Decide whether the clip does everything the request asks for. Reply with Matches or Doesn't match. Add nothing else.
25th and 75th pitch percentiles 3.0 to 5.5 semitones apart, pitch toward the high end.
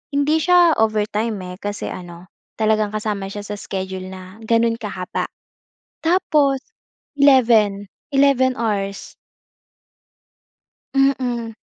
Matches